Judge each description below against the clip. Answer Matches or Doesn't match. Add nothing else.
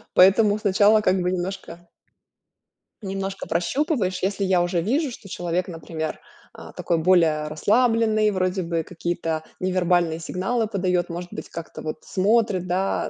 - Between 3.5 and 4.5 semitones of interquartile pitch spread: Doesn't match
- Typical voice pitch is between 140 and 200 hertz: Matches